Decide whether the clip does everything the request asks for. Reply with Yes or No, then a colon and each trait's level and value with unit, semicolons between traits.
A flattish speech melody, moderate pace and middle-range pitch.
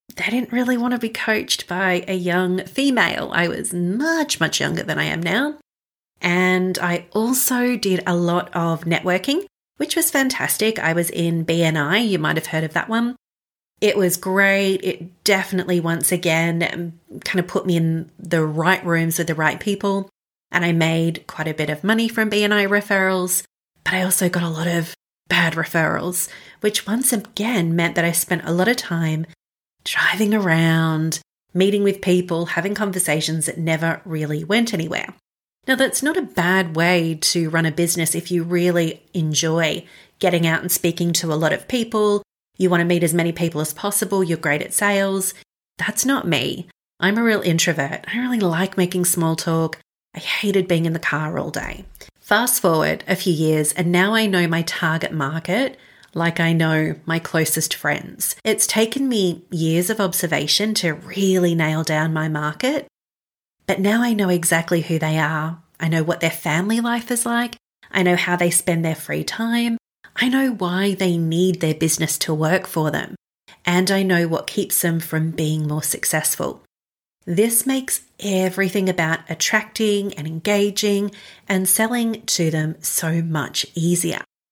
No: average, 3.7 semitones; average, 175 wpm; medium, 180 Hz